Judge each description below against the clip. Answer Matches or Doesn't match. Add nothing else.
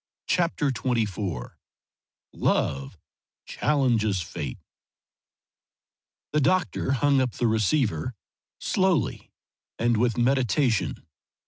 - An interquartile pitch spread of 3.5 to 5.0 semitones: Matches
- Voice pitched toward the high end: Doesn't match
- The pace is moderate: Doesn't match